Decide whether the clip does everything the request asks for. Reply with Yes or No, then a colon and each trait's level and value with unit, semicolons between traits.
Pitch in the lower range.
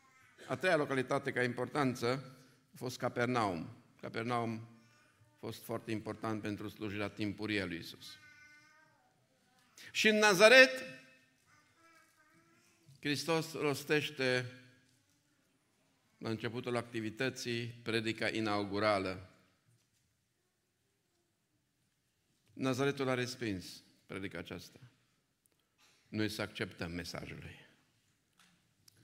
Yes: low, 125 Hz